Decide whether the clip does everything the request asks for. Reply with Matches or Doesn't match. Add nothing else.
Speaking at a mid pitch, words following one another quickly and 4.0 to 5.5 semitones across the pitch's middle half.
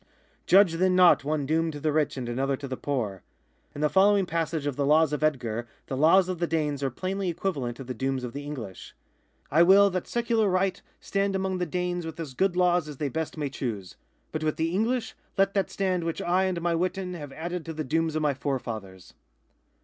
Matches